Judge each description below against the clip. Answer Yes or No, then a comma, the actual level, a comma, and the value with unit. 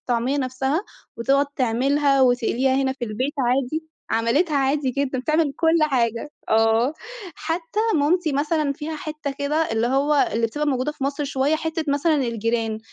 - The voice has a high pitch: Yes, very high, 275 Hz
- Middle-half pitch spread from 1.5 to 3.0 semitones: No, average, 3.4 semitones